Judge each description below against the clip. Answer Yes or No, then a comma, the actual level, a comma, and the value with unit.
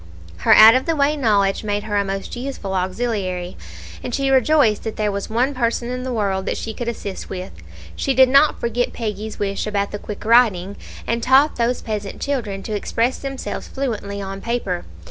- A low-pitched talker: No, high, 220 Hz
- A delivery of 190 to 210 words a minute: Yes, average, 200 wpm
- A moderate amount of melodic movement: Yes, average, 3.9 semitones